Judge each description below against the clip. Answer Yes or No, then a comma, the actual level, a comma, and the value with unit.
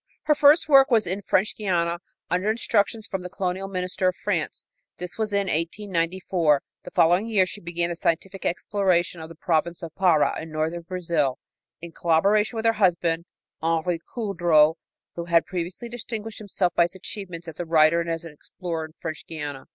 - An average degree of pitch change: Yes, average, 3.2 semitones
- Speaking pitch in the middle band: Yes, medium, 175 Hz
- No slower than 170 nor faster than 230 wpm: Yes, average, 180 wpm